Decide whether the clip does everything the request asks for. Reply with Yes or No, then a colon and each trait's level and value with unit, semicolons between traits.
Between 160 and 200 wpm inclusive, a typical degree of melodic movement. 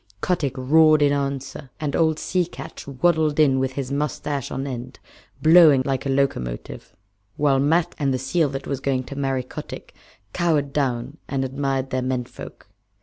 No: average, 170 wpm; narrow, 2.2 semitones